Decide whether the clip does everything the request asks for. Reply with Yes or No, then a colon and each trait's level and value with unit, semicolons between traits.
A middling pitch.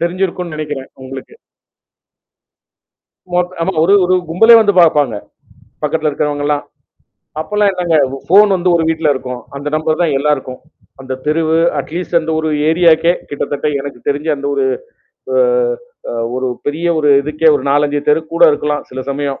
Yes: medium, 155 Hz